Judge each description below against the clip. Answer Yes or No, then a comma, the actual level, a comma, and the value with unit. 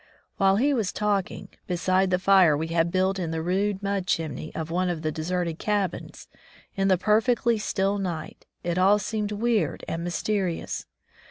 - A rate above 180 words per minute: No, average, 170 wpm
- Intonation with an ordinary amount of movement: Yes, average, 3.1 semitones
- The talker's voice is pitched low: No, high, 190 Hz